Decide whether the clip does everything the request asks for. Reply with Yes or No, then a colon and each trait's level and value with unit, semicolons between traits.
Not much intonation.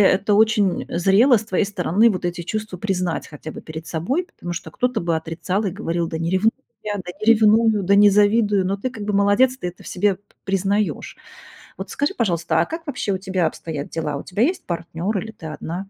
No: average, 3.8 semitones